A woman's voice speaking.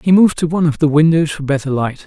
No: male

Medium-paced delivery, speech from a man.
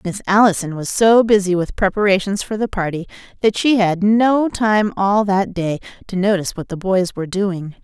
No: average, 190 wpm; female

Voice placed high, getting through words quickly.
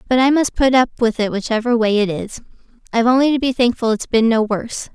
Yes: high, 235 Hz; fast, 230 wpm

